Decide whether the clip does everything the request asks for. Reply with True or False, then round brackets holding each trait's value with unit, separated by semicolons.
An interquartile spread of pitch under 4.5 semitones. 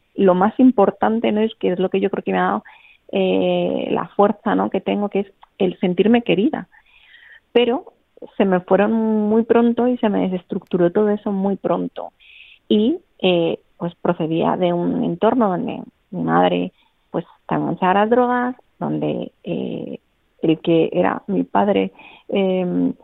False (5.0 semitones)